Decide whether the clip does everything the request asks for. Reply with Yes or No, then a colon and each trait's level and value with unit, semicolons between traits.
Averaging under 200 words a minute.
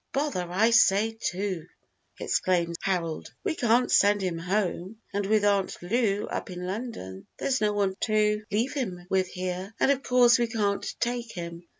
Yes: average, 170 wpm